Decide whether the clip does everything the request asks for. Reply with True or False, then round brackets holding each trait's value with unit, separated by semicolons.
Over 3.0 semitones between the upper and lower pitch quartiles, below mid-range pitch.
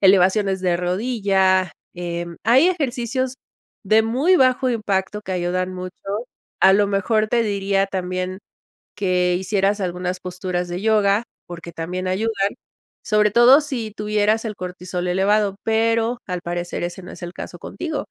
False (3.4 semitones; 195 Hz)